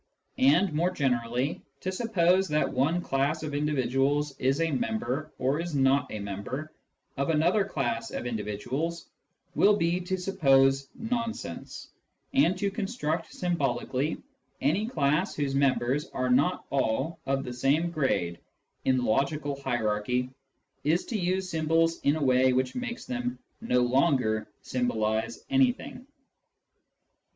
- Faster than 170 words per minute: No, slow, 135 wpm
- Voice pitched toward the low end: No, medium, 145 Hz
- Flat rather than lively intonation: No, average, 5.1 semitones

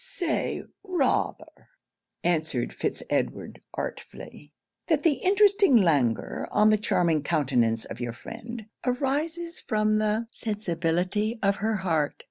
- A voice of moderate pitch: No, high, 215 Hz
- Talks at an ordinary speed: No, slow, 115 wpm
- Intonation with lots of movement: Yes, wide, 8.6 semitones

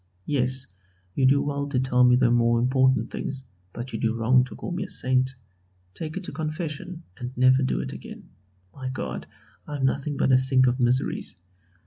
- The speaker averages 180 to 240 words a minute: Yes, average, 195 wpm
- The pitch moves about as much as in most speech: No, narrow, 2.3 semitones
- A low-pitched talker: Yes, low, 130 Hz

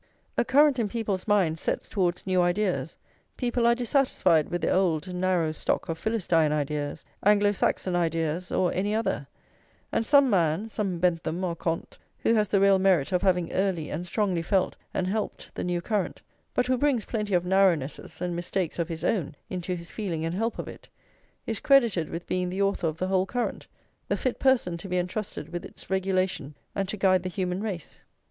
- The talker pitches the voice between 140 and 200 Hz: Yes, medium, 185 Hz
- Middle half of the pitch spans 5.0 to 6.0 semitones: No, average, 3.4 semitones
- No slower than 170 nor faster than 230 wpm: Yes, average, 195 wpm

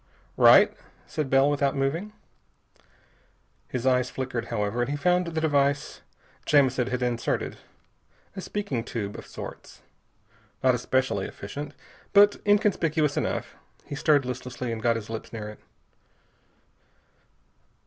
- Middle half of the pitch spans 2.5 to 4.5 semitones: Yes, average, 3.8 semitones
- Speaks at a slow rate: Yes, slow, 125 wpm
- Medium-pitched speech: No, low, 130 Hz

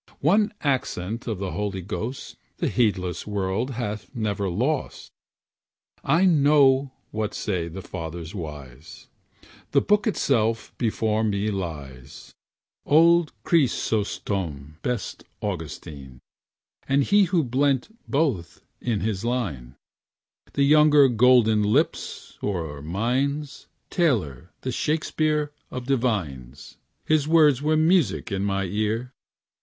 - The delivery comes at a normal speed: No, slow, 110 wpm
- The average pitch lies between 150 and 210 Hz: No, low, 110 Hz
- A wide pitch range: Yes, wide, 7.1 semitones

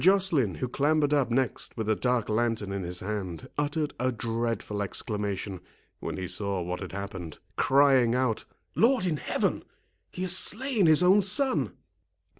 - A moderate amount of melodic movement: No, wide, 7.4 semitones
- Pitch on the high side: No, low, 120 Hz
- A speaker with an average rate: Yes, average, 160 wpm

